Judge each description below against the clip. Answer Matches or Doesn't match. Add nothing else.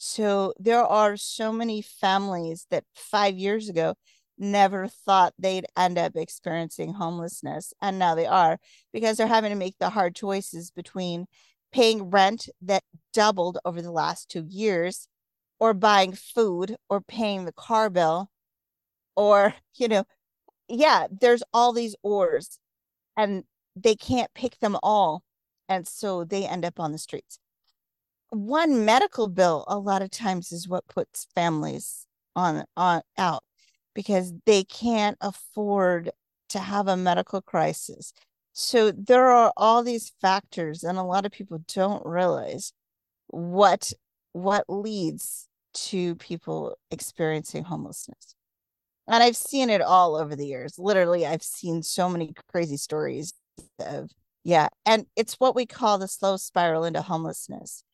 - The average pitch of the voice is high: Matches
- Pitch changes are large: Doesn't match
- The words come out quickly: Doesn't match